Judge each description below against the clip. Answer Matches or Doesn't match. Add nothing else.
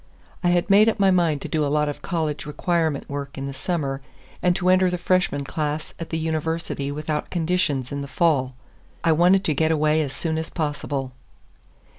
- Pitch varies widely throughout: Doesn't match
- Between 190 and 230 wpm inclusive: Matches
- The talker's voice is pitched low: Doesn't match